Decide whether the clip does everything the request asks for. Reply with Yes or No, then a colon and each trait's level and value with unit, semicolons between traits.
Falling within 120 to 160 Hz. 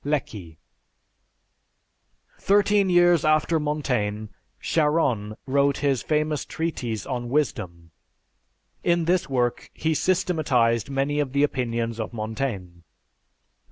Yes: medium, 140 Hz